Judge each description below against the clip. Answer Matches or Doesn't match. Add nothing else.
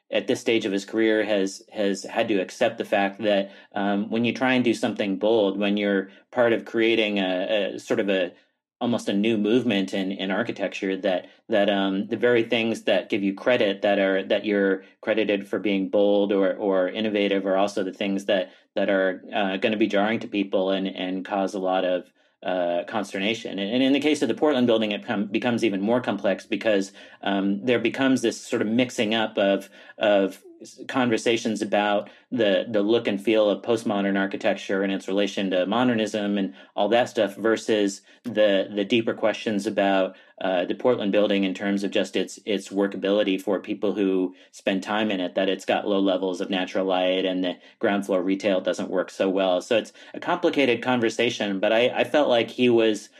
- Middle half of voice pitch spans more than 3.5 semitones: Doesn't match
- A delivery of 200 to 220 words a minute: Matches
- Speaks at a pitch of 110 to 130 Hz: Doesn't match